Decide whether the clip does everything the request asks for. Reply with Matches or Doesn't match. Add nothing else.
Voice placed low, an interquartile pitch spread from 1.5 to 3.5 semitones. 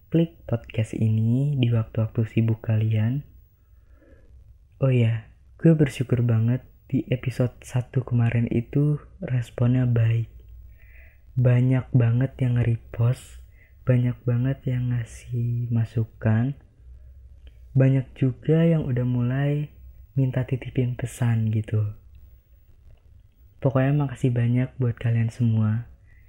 Matches